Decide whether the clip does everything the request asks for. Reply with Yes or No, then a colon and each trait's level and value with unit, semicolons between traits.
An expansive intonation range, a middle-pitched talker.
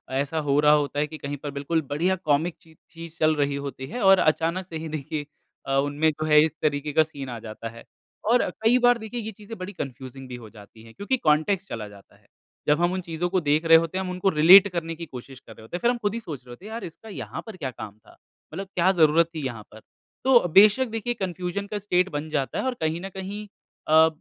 No: average, 4.9 semitones; medium, 160 Hz